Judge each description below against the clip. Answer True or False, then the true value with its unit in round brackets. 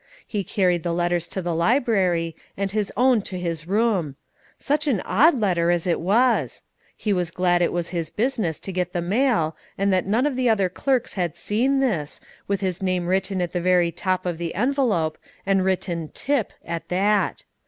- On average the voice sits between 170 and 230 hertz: True (185 Hz)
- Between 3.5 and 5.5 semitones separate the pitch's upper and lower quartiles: True (4.0 semitones)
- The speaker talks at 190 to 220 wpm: True (195 wpm)